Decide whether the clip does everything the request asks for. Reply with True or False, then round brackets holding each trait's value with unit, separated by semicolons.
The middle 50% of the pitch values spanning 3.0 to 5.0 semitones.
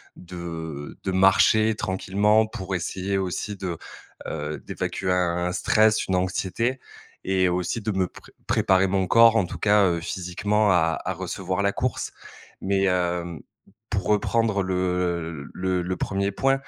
False (2.5 semitones)